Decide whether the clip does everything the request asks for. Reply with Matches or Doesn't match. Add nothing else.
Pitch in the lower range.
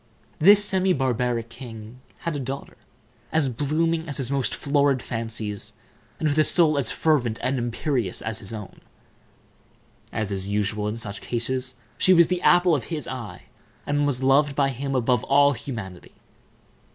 Matches